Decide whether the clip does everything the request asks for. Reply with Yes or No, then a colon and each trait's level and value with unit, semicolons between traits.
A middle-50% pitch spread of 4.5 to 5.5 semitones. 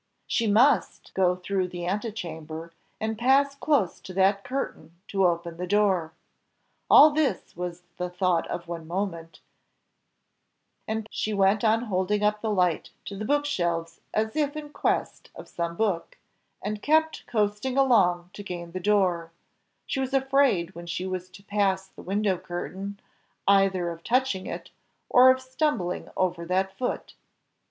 No: average, 4.0 semitones